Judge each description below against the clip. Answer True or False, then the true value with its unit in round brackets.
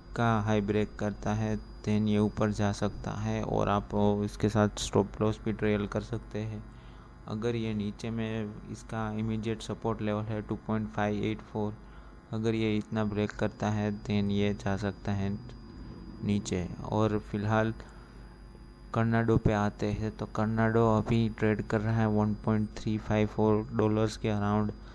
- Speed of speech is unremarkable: True (165 wpm)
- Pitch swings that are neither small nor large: False (1.1 semitones)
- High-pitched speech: False (105 Hz)